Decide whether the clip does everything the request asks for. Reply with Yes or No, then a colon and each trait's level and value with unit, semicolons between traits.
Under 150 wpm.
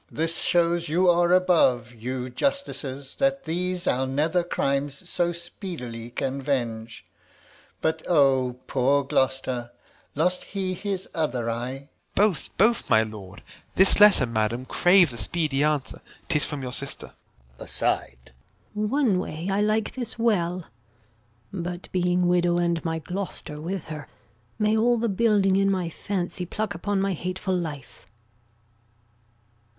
Yes: average, 140 wpm